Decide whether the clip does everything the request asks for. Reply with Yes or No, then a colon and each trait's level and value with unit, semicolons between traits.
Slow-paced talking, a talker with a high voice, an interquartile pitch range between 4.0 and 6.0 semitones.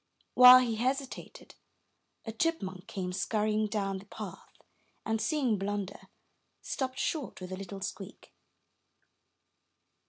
Yes: slow, 115 wpm; high, 215 Hz; average, 4.4 semitones